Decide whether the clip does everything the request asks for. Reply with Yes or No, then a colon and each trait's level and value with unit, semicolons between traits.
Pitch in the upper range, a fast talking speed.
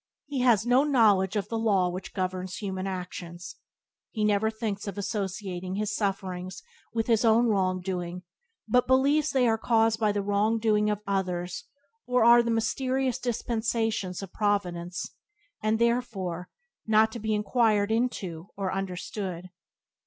No: high, 210 Hz; average, 150 wpm